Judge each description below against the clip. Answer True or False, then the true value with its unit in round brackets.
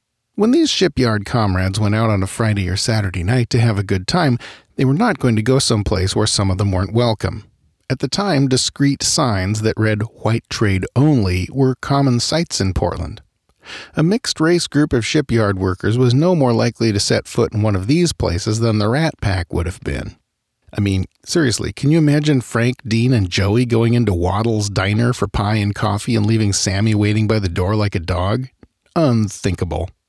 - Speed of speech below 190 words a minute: False (200 wpm)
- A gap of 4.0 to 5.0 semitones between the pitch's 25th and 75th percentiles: True (4.3 semitones)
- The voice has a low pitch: True (110 Hz)